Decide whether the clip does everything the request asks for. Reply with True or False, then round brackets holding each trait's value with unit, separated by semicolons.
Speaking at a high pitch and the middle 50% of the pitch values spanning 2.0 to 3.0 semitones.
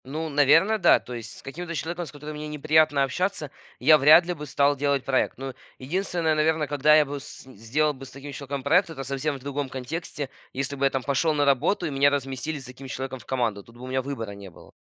False (140 Hz; 2.6 semitones)